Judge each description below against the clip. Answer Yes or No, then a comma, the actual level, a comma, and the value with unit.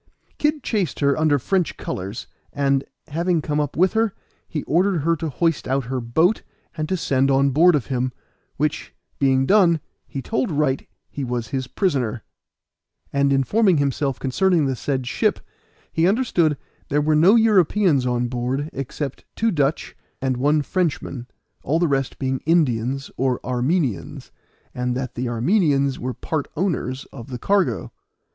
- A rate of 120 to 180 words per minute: Yes, average, 160 wpm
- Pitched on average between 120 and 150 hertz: Yes, medium, 140 Hz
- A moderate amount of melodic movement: Yes, average, 4.5 semitones